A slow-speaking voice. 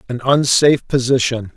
Yes: slow, 115 wpm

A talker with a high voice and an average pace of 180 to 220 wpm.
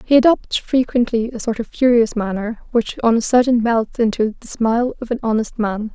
Yes: high, 230 Hz; average, 200 wpm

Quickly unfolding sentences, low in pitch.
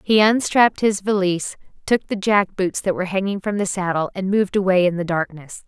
No: fast, 210 wpm; high, 190 Hz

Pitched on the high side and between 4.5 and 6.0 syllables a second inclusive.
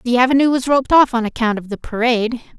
No: high, 245 Hz; 6.8 syllables/s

